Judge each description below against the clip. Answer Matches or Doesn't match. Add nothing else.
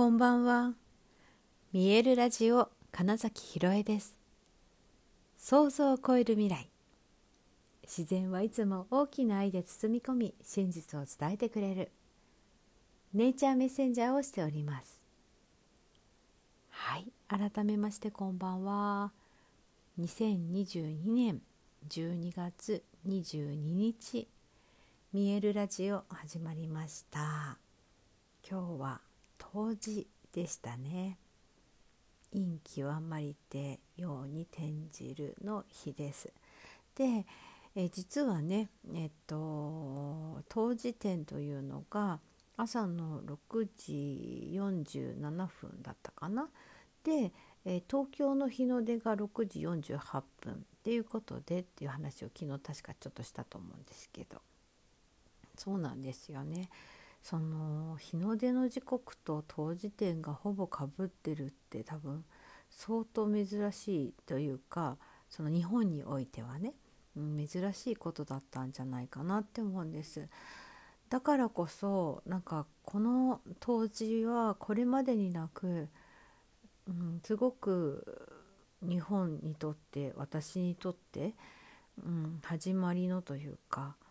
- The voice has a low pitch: Doesn't match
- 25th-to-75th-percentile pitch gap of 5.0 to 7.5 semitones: Matches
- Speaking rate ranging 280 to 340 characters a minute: Doesn't match